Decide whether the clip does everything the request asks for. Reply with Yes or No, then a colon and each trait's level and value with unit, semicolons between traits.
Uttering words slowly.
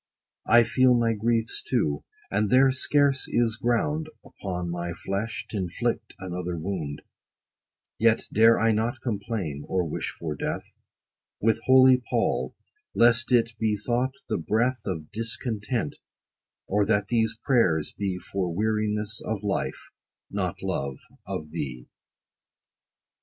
Yes: slow, 130 wpm